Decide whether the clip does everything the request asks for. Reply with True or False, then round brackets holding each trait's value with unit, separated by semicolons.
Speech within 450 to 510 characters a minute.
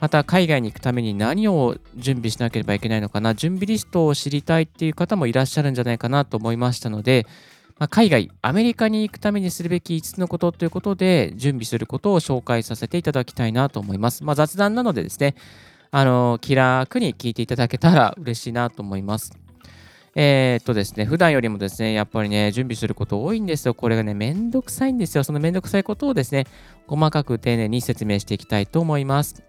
True (465 characters per minute)